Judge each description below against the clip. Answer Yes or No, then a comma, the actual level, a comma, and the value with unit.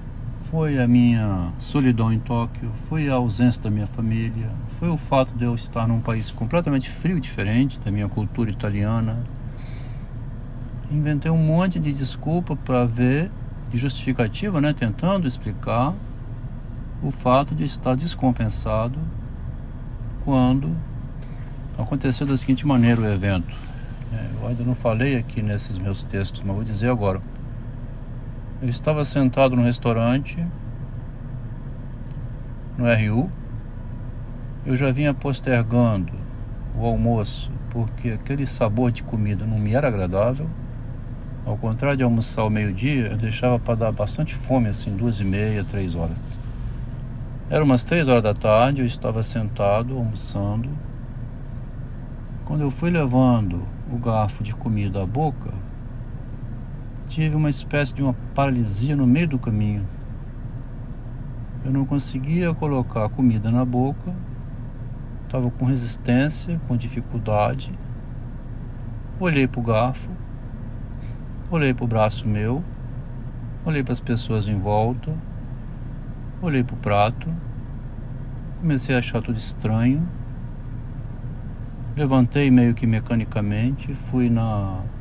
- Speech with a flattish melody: Yes, narrow, 2.0 semitones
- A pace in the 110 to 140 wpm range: Yes, average, 125 wpm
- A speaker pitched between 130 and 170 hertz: No, low, 120 Hz